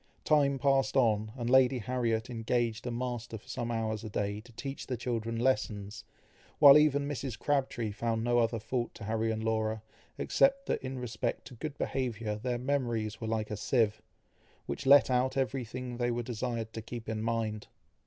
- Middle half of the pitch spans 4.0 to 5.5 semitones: No, average, 2.7 semitones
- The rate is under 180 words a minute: No, average, 185 wpm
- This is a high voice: No, low, 120 Hz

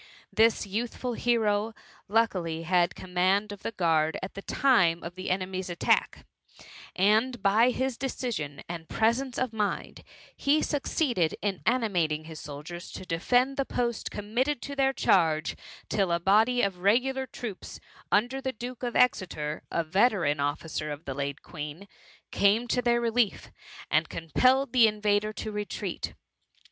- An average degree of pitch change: No, wide, 6.0 semitones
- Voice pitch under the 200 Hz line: No, high, 205 Hz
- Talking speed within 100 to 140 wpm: No, average, 155 wpm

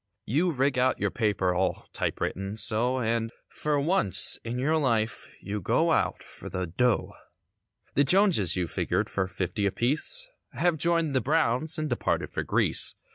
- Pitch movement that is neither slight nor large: No, wide, 6.8 semitones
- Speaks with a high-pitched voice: No, low, 125 Hz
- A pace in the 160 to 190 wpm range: Yes, average, 170 wpm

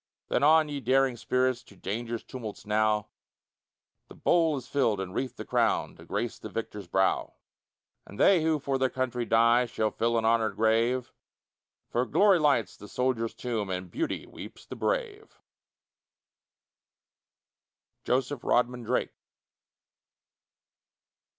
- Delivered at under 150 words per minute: Yes, slow, 135 wpm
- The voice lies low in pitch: Yes, low, 125 Hz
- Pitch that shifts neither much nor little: Yes, average, 3.4 semitones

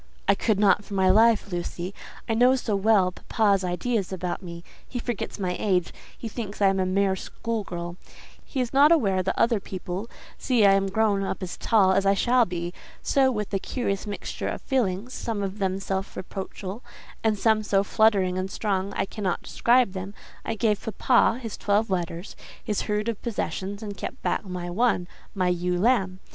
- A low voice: No, high, 200 Hz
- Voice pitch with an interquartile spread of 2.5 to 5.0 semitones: Yes, average, 3.0 semitones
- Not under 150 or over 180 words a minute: No, average, 190 wpm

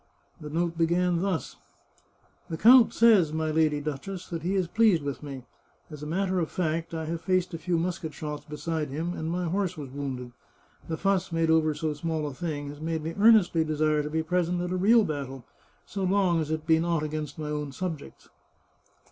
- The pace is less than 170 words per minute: No, fast, 205 wpm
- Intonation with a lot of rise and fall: No, average, 2.9 semitones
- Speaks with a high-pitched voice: No, medium, 160 Hz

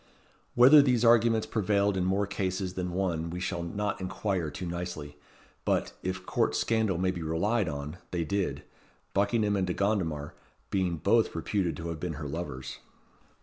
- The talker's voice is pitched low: Yes, very low, 95 Hz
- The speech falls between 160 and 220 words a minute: Yes, average, 165 wpm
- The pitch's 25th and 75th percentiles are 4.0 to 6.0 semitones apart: No, average, 3.4 semitones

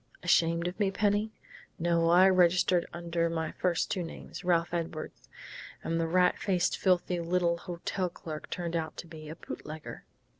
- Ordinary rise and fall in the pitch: No, narrow, 1.5 semitones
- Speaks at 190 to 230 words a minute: No, average, 160 wpm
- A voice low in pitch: No, medium, 170 Hz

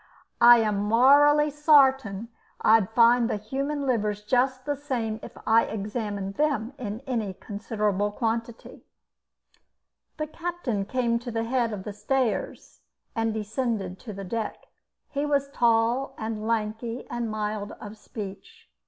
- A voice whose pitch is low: No, high, 230 Hz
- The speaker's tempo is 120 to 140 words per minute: Yes, slow, 135 wpm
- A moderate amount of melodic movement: Yes, average, 3.5 semitones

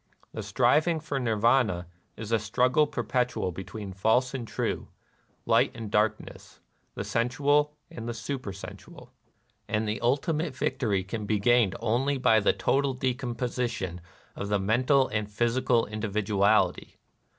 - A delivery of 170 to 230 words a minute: No, average, 140 wpm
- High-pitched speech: No, low, 115 Hz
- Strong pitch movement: No, average, 3.5 semitones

